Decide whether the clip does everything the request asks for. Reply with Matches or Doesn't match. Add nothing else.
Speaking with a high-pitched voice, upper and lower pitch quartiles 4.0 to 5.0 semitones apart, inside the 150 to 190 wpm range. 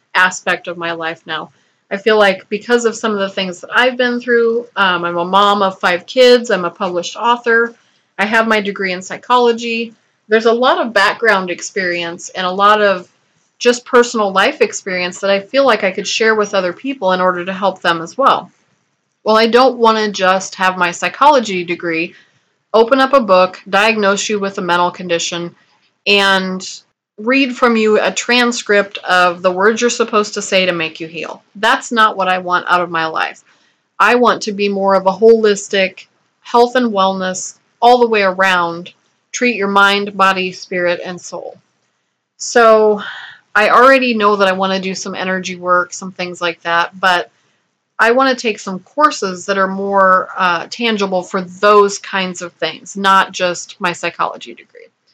Doesn't match